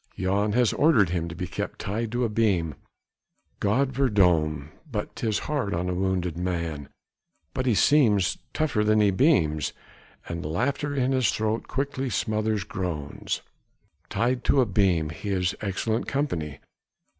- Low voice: Yes, low, 105 Hz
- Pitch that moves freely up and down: Yes, wide, 5.8 semitones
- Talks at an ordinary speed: Yes, average, 150 wpm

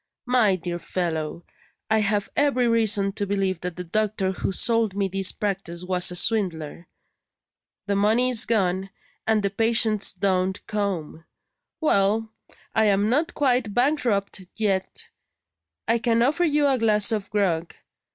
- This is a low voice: No, high, 205 Hz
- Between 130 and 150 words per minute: Yes, average, 145 wpm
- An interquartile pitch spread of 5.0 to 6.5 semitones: No, average, 3.3 semitones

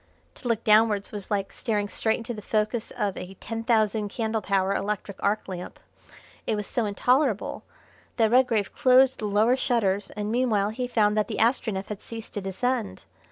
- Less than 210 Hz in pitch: No, high, 215 Hz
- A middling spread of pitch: No, narrow, 2.3 semitones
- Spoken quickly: No, average, 180 wpm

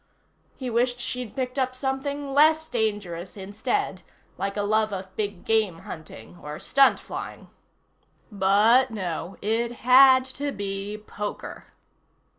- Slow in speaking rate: Yes, slow, 125 wpm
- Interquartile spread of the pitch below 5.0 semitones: Yes, average, 4.6 semitones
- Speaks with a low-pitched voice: No, high, 220 Hz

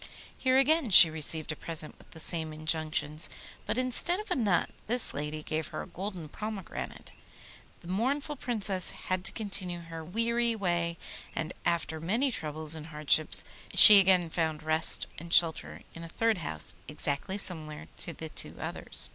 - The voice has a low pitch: No, medium, 170 Hz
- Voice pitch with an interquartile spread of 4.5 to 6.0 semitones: Yes, average, 5.2 semitones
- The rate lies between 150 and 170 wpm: Yes, average, 165 wpm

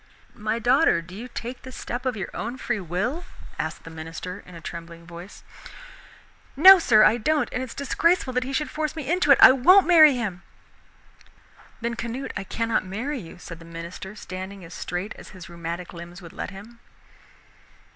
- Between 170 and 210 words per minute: Yes, average, 185 wpm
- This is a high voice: Yes, high, 215 Hz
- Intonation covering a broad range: Yes, wide, 6.7 semitones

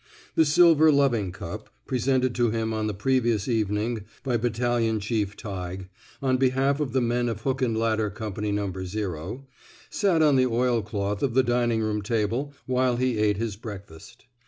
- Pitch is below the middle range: Yes, low, 115 Hz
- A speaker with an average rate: Yes, average, 170 wpm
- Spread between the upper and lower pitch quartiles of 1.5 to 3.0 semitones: No, average, 3.5 semitones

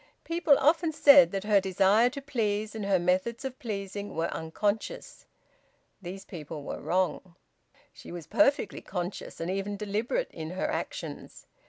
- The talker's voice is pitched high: Yes, high, 205 Hz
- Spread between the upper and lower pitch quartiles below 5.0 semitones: No, average, 5.3 semitones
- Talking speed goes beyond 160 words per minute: No, average, 150 wpm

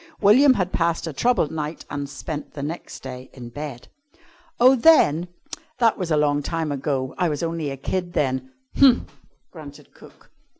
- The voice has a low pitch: No, medium, 155 Hz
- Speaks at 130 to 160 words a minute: No, average, 170 wpm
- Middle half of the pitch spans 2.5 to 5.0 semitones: Yes, average, 4.1 semitones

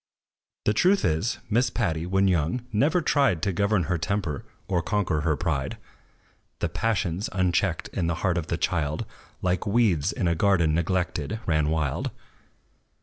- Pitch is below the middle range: Yes, very low, 90 Hz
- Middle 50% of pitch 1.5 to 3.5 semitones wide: No, average, 4.4 semitones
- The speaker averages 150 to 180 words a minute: Yes, average, 155 wpm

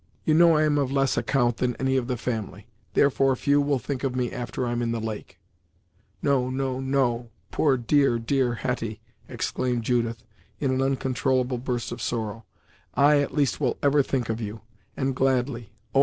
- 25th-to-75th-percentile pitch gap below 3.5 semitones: Yes, narrow, 2.4 semitones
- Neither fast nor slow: Yes, average, 185 wpm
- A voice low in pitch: Yes, low, 130 Hz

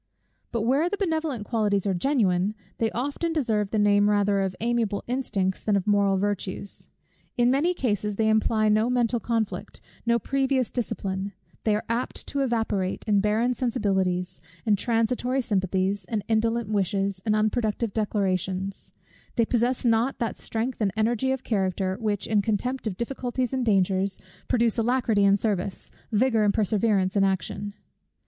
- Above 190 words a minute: No, average, 155 wpm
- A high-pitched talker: Yes, high, 215 Hz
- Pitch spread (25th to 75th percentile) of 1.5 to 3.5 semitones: Yes, average, 3.2 semitones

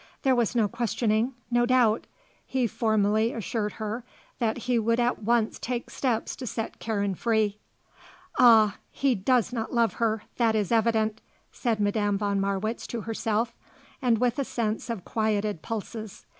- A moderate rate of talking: Yes, average, 155 wpm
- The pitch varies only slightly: Yes, narrow, 2.0 semitones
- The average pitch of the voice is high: Yes, high, 225 Hz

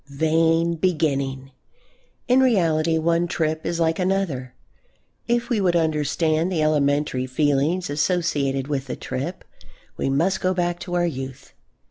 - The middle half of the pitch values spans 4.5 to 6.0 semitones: No, average, 3.6 semitones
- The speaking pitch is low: No, medium, 160 Hz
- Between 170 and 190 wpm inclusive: No, slow, 135 wpm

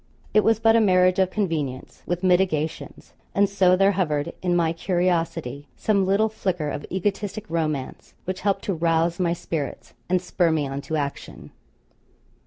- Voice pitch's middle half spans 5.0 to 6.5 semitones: No, average, 3.4 semitones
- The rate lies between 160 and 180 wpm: Yes, average, 165 wpm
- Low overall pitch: No, medium, 180 Hz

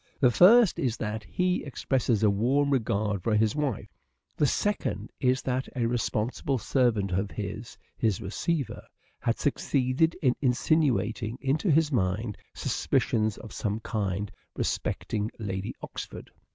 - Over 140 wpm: No, slow, 135 wpm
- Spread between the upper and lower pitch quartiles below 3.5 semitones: No, average, 4.5 semitones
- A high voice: No, low, 120 Hz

